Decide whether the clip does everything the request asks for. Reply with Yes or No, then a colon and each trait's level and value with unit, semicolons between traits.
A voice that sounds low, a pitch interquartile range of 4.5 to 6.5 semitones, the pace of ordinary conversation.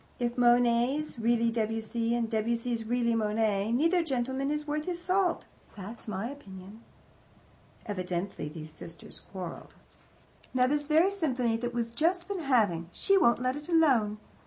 No: high, 235 Hz; average, 5.2 semitones; average, 145 wpm